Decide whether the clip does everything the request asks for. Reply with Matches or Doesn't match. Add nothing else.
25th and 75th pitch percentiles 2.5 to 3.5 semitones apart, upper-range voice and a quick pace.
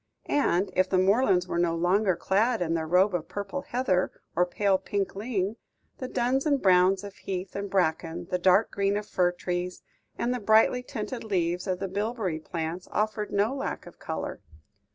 Doesn't match